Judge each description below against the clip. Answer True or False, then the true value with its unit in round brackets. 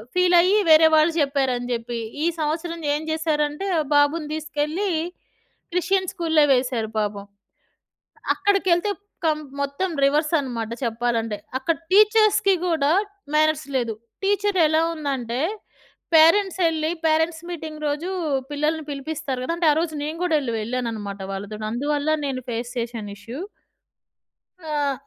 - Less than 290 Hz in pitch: False (305 Hz)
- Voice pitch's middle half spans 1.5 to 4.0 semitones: False (4.9 semitones)